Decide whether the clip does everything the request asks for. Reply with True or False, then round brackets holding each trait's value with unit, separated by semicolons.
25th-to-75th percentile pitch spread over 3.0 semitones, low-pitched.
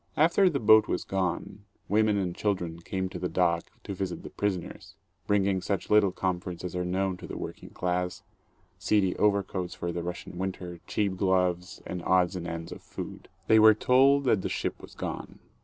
False (2.4 semitones; 95 Hz)